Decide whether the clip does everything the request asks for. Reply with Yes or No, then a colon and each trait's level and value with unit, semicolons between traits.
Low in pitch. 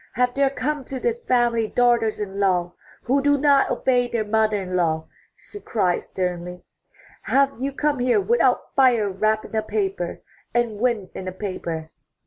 No: high, 230 Hz